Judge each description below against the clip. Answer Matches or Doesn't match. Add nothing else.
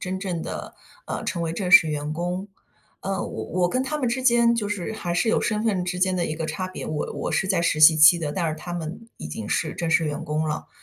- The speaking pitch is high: Doesn't match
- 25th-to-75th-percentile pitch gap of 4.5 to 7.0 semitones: Doesn't match